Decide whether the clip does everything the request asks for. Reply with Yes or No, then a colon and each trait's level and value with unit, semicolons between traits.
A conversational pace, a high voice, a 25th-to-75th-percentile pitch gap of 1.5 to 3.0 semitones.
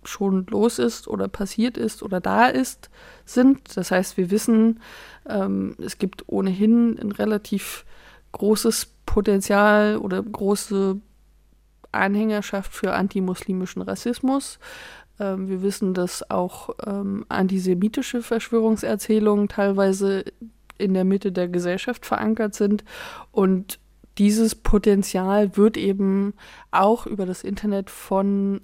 No: slow, 115 wpm; high, 205 Hz; narrow, 2.4 semitones